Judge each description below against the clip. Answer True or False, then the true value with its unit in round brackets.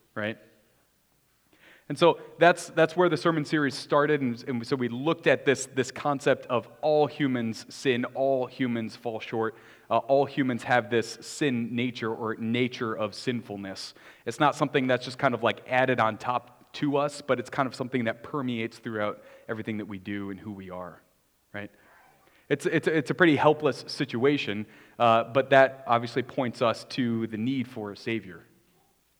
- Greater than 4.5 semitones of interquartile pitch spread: False (3.7 semitones)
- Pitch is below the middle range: True (120 Hz)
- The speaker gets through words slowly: False (180 wpm)